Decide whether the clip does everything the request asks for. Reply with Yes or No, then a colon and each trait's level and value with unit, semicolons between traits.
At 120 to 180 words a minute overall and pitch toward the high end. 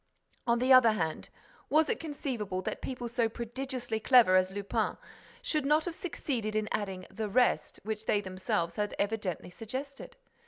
Yes: average, 160 wpm; high, 225 Hz